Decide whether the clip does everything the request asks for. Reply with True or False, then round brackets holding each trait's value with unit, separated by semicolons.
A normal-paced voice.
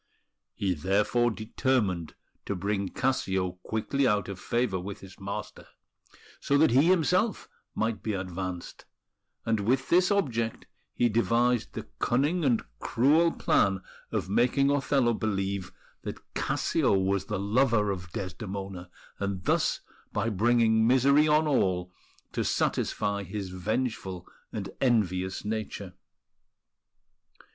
False (120 wpm)